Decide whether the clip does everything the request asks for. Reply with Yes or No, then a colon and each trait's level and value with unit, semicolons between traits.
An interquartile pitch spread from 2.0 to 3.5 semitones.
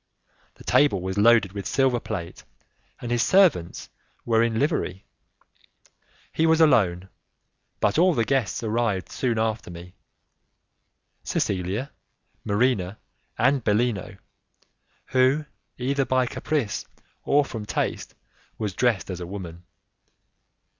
No: wide, 5.4 semitones